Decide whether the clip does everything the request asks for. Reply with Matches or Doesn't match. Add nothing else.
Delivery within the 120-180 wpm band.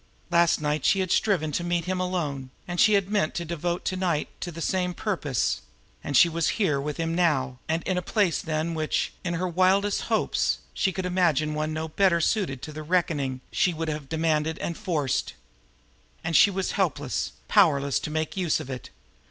Doesn't match